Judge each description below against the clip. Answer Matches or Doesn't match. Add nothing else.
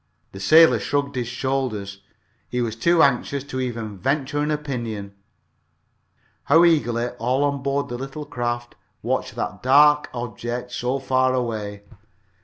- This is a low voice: Matches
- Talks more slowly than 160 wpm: Matches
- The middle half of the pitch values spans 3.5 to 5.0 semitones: Doesn't match